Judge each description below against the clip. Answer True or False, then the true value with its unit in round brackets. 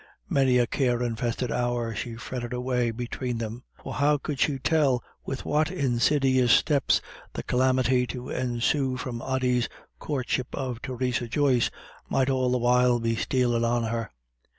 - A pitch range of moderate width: False (1.6 semitones)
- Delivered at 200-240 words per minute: False (150 wpm)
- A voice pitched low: True (125 Hz)